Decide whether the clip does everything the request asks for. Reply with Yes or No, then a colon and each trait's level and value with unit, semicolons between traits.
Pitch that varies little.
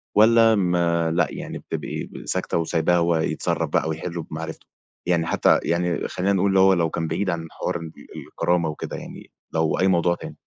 Yes: narrow, 1.8 semitones